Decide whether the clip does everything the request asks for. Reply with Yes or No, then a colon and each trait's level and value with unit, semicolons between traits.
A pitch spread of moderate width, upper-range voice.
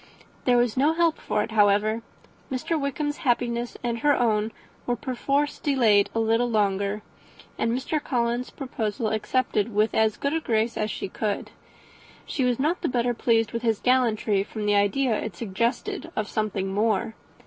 Yes: average, 3.2 semitones; high, 230 Hz